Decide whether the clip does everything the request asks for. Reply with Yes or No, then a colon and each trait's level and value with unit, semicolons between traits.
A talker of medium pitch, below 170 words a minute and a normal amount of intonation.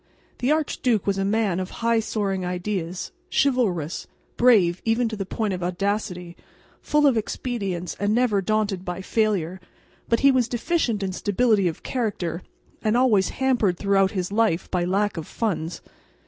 No: high, 205 Hz; average, 160 wpm; average, 4.1 semitones